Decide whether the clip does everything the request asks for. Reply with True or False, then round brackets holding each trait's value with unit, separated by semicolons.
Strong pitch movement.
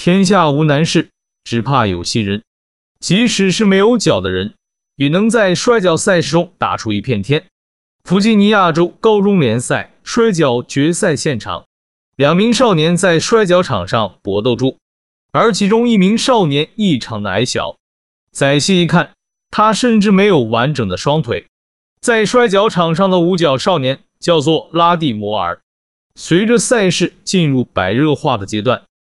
True (9.0 semitones)